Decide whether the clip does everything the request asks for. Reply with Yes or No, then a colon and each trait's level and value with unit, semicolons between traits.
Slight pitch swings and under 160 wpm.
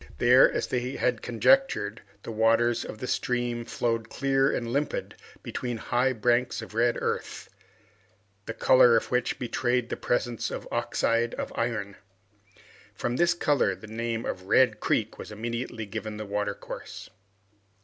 Yes: narrow, 1.9 semitones; average, 150 wpm